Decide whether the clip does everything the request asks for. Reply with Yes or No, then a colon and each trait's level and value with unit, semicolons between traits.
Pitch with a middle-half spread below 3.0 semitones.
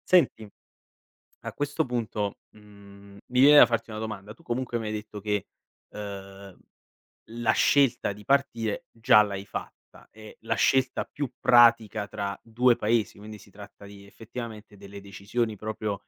Yes: narrow, 2.6 semitones